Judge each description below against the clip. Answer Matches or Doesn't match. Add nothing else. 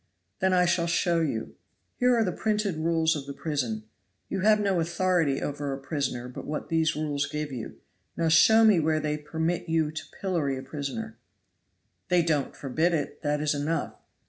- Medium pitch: Matches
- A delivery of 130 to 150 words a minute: Doesn't match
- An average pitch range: Matches